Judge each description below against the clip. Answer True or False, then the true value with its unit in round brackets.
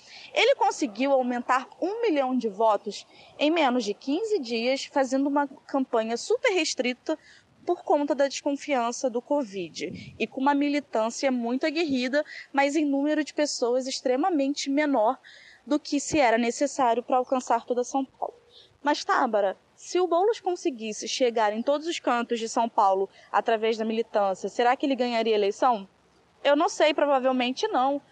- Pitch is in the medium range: False (270 Hz)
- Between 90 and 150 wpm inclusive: False (160 wpm)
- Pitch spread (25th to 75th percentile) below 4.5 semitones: True (4.1 semitones)